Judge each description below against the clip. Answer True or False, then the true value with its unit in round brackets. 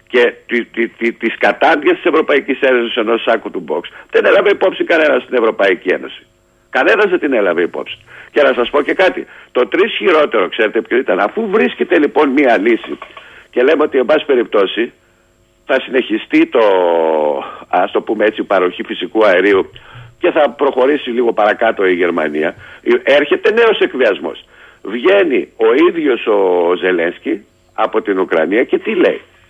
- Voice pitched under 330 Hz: False (375 Hz)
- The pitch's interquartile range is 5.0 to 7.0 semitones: True (5.5 semitones)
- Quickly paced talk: False (155 wpm)